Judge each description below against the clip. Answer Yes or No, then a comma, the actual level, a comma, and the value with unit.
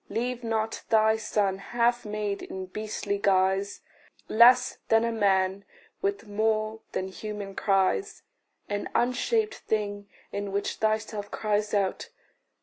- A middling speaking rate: No, slow, 125 wpm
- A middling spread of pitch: No, narrow, 1.9 semitones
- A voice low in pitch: No, high, 215 Hz